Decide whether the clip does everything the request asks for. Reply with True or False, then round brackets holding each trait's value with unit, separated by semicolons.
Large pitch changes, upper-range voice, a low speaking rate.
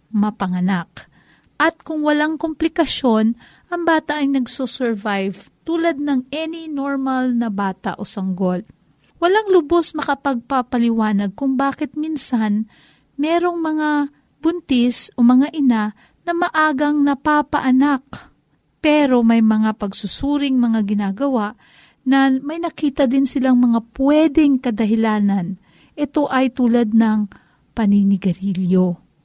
True (5.8 semitones; 260 Hz; 105 wpm)